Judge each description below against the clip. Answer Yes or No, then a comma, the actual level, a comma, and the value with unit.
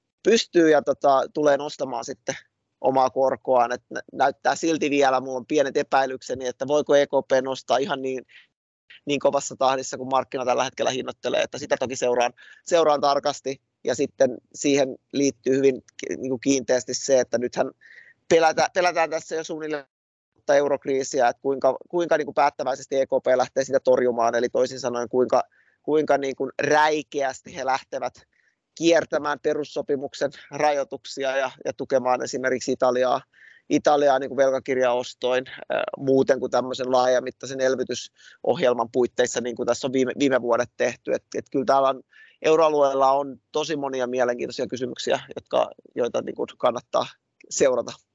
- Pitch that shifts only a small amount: Yes, narrow, 2.0 semitones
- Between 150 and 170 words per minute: No, average, 140 wpm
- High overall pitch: No, low, 135 Hz